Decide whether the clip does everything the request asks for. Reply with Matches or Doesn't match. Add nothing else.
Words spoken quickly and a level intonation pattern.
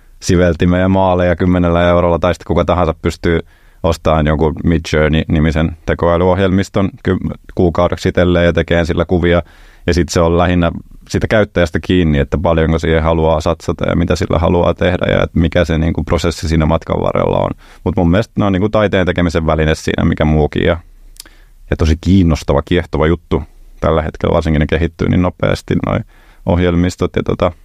Matches